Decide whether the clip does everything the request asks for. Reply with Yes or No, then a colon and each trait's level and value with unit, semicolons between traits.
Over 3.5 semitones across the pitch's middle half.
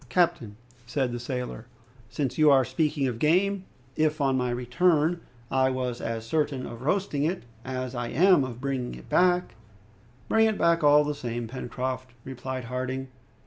Yes: average, 3.9 semitones